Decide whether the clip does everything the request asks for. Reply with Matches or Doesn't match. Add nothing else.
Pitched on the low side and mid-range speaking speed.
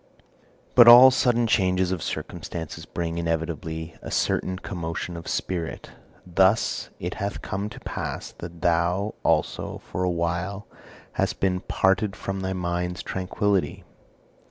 Doesn't match